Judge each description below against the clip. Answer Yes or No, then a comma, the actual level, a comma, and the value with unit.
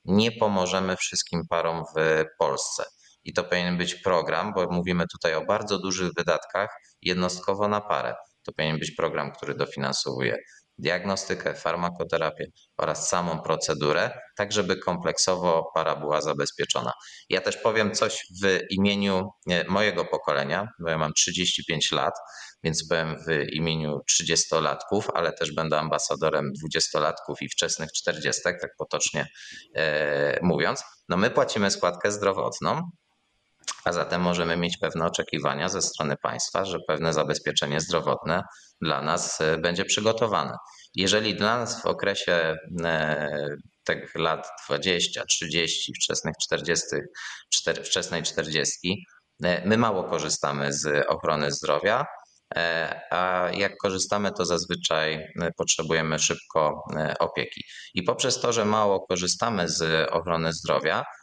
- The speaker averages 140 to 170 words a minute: No, average, 125 wpm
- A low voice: Yes, very low, 85 Hz